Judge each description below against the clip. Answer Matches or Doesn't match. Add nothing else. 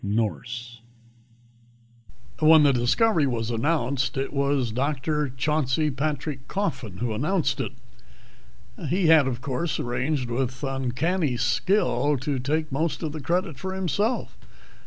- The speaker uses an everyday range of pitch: Matches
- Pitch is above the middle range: Doesn't match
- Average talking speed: Doesn't match